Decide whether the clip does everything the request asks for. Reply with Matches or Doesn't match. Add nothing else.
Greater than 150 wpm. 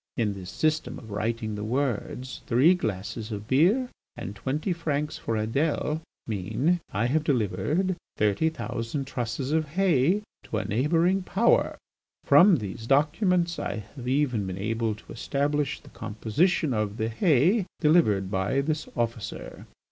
Doesn't match